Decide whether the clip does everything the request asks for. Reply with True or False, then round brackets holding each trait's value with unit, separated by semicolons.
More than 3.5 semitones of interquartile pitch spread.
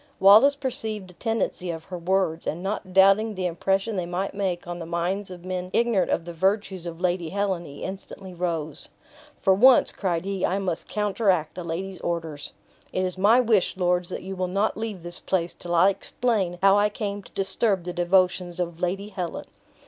False (2.4 semitones)